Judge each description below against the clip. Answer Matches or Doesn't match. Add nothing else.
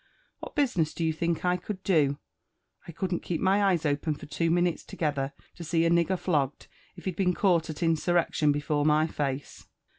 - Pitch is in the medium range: Matches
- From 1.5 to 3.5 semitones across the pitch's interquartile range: Matches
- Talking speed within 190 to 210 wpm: Matches